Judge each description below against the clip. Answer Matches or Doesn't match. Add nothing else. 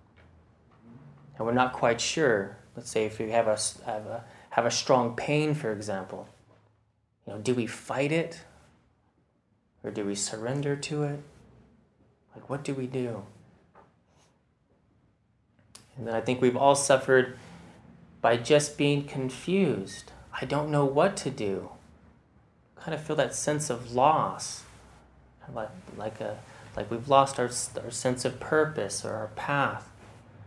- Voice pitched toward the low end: Matches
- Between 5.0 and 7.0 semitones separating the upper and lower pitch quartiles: Doesn't match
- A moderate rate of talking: Matches